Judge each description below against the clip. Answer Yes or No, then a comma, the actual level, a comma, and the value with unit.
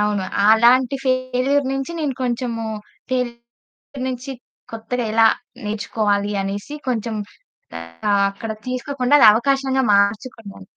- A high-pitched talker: Yes, high, 240 Hz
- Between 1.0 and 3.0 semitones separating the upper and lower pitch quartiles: No, average, 3.5 semitones